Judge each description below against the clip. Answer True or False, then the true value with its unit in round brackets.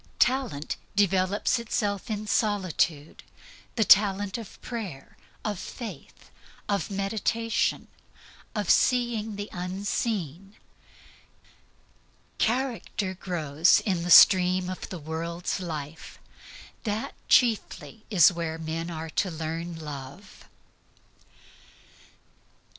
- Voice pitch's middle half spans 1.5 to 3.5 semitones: False (4.2 semitones)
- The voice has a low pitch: False (190 Hz)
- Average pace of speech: False (90 wpm)